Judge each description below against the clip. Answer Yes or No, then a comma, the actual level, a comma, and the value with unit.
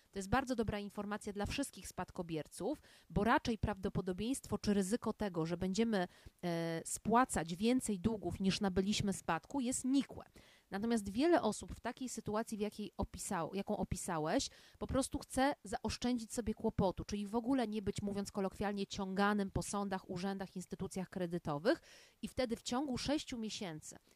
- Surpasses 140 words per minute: Yes, average, 150 wpm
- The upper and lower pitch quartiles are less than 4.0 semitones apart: Yes, average, 3.5 semitones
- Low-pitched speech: No, high, 205 Hz